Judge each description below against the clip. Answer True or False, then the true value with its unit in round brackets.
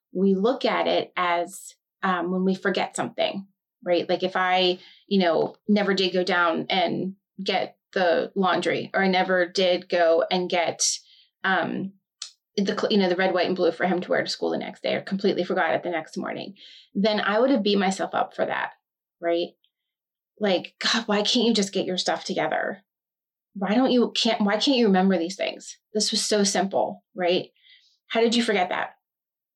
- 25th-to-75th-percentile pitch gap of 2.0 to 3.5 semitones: True (3.2 semitones)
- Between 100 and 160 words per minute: False (195 wpm)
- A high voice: True (195 Hz)